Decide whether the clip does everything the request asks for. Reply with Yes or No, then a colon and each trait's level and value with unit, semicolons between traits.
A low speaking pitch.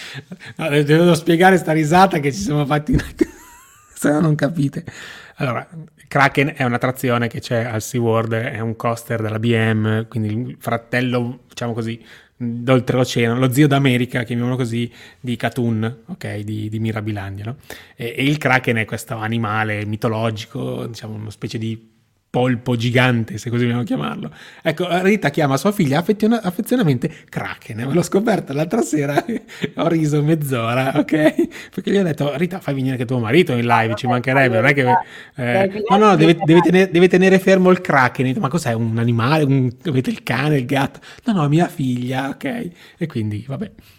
Yes: low, 130 Hz